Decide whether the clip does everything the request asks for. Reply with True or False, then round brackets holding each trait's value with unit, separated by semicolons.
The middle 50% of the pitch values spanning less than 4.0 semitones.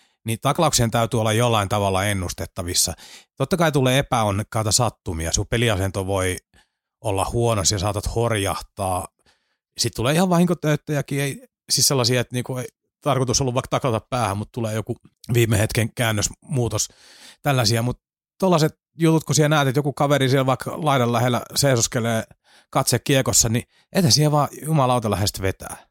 False (4.5 semitones)